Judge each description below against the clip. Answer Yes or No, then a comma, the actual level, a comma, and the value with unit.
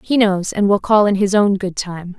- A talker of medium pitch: No, high, 200 Hz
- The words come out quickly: Yes, fast, 275 wpm